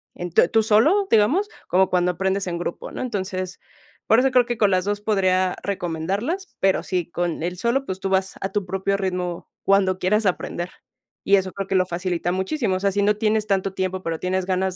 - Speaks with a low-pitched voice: No, high, 190 Hz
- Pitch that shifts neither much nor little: No, narrow, 2.2 semitones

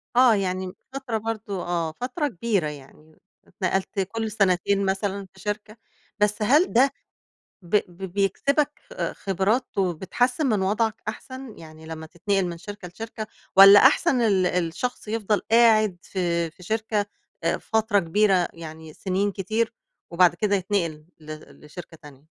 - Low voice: No, high, 200 Hz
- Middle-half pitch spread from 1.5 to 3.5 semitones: No, average, 4.0 semitones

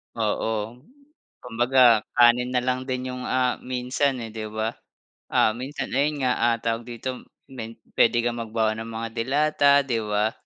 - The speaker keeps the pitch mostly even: Yes, narrow, 2.1 semitones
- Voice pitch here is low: Yes, low, 120 Hz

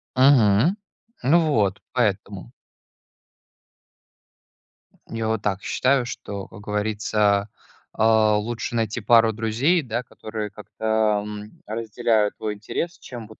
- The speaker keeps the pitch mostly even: Yes, narrow, 2.2 semitones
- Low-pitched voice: Yes, low, 110 Hz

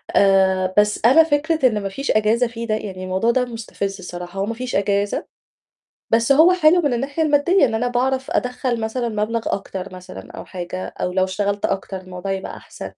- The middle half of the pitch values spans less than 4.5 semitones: No, average, 4.8 semitones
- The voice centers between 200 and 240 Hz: Yes, high, 220 Hz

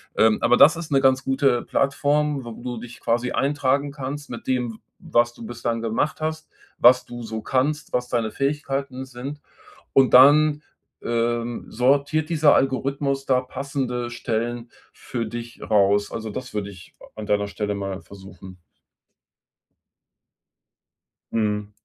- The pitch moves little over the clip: No, average, 3.2 semitones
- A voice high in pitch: No, low, 125 Hz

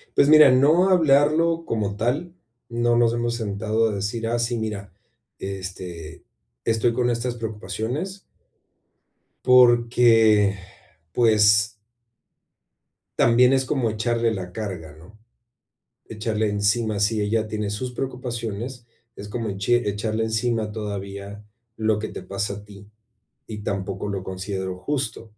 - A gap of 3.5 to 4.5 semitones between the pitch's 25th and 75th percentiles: No, average, 2.8 semitones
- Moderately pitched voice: No, low, 110 Hz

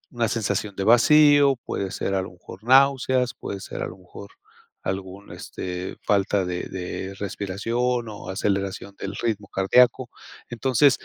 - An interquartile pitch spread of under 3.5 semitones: No, average, 4.3 semitones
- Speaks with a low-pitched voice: Yes, low, 100 Hz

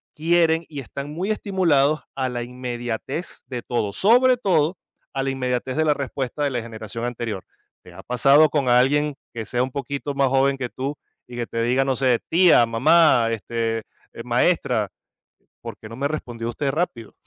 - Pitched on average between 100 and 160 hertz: Yes, low, 135 Hz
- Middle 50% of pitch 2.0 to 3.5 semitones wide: No, average, 3.9 semitones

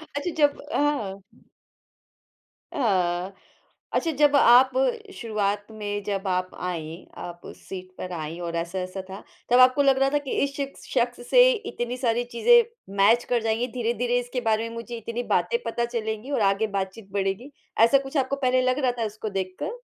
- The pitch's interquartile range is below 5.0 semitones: No, average, 5.3 semitones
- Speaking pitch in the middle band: No, high, 230 Hz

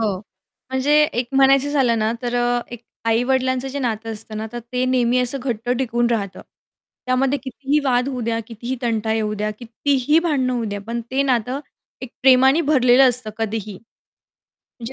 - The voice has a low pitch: No, high, 245 Hz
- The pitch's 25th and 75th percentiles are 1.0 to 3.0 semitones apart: Yes, average, 2.7 semitones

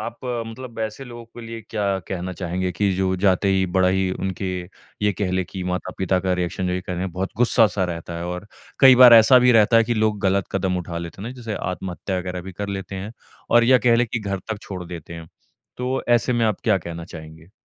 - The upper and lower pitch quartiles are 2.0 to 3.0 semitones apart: No, average, 3.8 semitones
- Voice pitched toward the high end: No, very low, 95 Hz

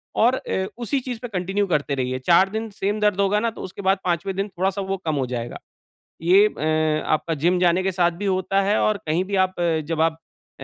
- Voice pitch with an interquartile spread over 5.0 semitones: No, average, 3.1 semitones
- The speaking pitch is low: No, high, 190 Hz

